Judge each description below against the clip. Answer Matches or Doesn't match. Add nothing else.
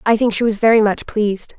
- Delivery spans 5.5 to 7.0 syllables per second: Matches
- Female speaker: Matches